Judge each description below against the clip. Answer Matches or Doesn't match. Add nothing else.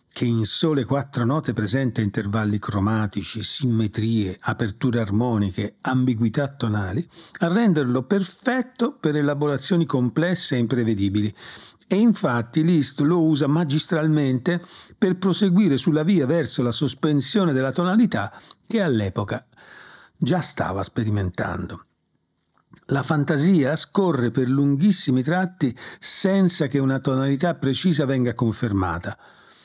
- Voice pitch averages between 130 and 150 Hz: Matches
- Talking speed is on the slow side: Matches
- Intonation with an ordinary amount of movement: Doesn't match